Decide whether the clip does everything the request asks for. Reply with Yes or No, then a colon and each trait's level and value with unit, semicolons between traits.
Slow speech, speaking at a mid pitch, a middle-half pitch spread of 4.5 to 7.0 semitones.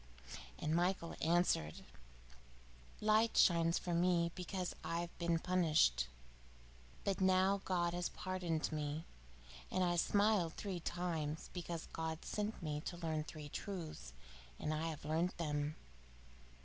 No: slow, 130 wpm; medium, 170 Hz; narrow, 2.6 semitones